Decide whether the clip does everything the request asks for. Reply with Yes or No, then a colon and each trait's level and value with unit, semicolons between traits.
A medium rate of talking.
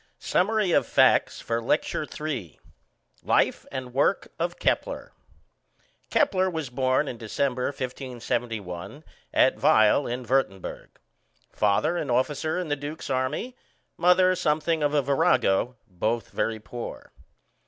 No: slow, 120 wpm